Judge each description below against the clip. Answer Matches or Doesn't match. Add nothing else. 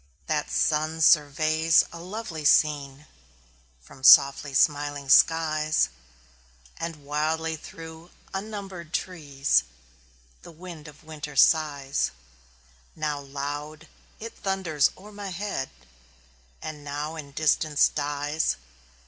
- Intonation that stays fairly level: Matches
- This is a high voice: Doesn't match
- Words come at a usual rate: Doesn't match